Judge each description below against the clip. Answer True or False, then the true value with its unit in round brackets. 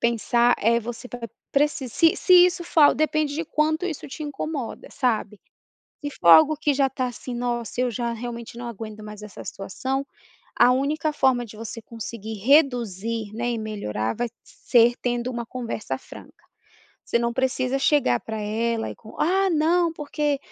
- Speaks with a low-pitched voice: False (245 Hz)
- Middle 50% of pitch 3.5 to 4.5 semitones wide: True (4.2 semitones)